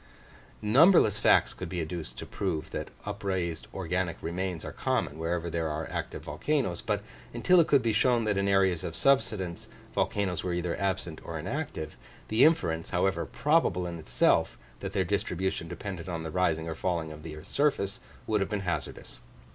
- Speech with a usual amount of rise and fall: Yes, average, 3.8 semitones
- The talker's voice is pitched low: Yes, very low, 90 Hz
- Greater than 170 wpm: Yes, average, 180 wpm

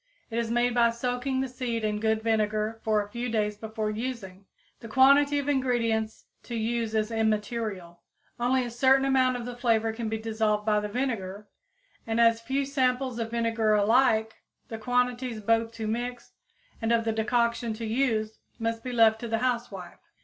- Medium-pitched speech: No, high, 230 Hz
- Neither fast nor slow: Yes, average, 185 wpm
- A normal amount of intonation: No, narrow, 2.2 semitones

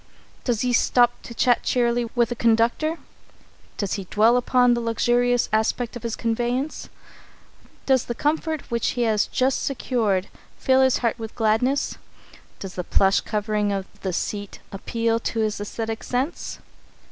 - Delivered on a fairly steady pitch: Yes, narrow, 2.3 semitones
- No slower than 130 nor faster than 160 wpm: Yes, average, 155 wpm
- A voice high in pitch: Yes, high, 235 Hz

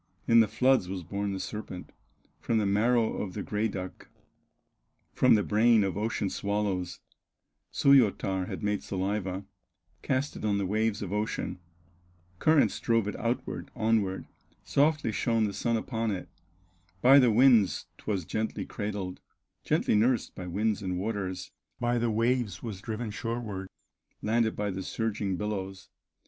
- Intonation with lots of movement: No, average, 3.0 semitones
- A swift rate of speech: No, average, 150 wpm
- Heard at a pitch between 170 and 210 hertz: No, low, 105 Hz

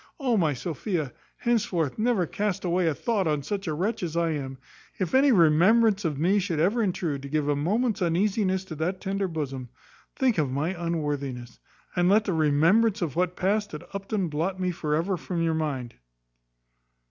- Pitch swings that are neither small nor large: Yes, average, 4.5 semitones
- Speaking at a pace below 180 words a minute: No, average, 185 wpm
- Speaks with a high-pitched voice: No, medium, 175 Hz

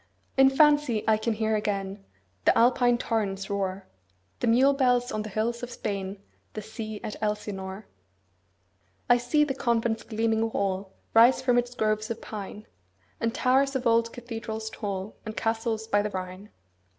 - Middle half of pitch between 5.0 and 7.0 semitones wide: No, average, 2.7 semitones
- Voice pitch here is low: No, high, 220 Hz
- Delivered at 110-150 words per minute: No, average, 165 wpm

